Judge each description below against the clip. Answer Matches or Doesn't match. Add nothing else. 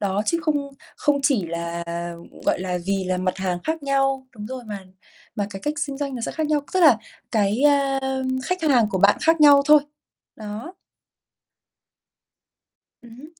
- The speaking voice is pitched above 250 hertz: Matches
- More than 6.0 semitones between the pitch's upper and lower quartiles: Matches